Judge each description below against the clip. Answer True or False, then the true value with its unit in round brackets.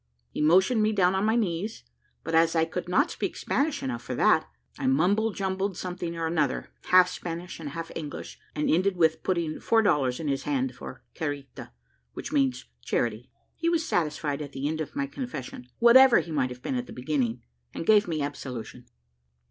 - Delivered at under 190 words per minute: False (195 wpm)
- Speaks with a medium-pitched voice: True (165 Hz)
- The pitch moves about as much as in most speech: False (5.7 semitones)